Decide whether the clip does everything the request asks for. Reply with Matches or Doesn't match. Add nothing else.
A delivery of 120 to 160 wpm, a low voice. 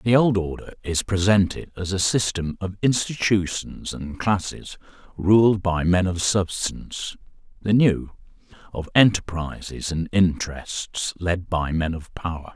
Matches